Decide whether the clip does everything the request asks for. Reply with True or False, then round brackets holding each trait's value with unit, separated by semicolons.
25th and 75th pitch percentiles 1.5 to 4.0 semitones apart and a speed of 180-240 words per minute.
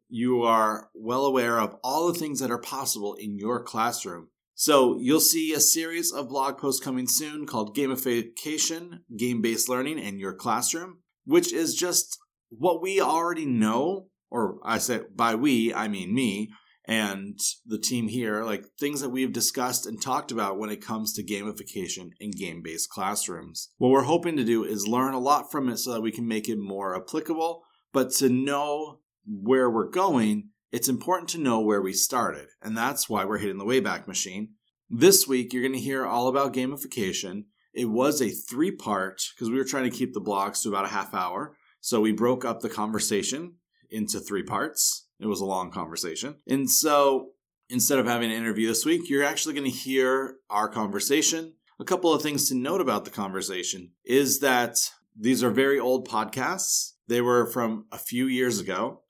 False (5.1 semitones; 190 wpm)